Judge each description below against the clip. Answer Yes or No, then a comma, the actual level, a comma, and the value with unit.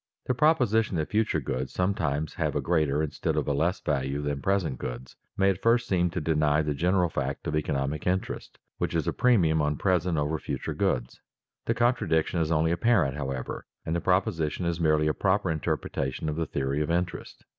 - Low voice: Yes, very low, 80 Hz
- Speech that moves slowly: No, average, 200 wpm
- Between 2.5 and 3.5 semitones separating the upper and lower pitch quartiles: No, average, 4.0 semitones